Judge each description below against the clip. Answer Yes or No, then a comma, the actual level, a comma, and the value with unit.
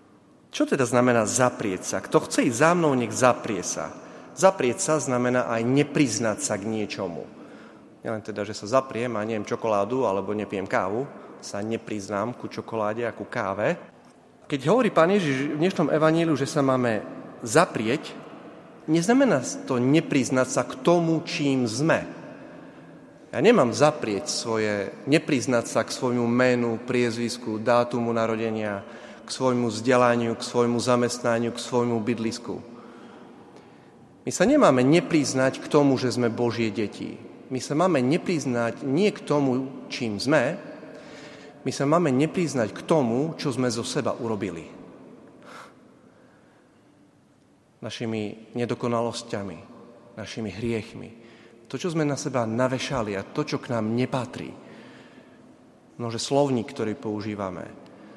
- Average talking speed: Yes, average, 135 wpm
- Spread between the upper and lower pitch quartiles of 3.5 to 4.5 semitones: Yes, average, 3.9 semitones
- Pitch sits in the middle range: No, low, 120 Hz